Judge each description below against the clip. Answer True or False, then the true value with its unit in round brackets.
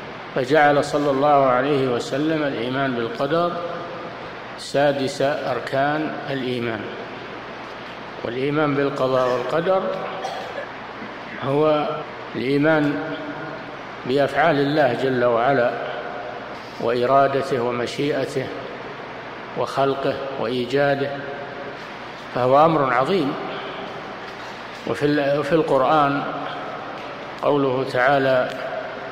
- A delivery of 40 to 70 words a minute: True (65 wpm)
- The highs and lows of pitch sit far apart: False (2.4 semitones)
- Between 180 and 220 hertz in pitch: False (140 Hz)